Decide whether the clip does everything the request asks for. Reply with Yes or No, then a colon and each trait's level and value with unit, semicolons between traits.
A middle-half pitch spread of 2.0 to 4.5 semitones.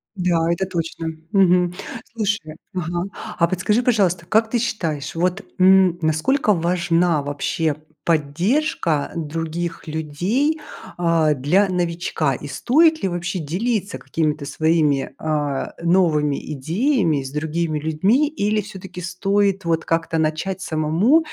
Yes: average, 3.7 semitones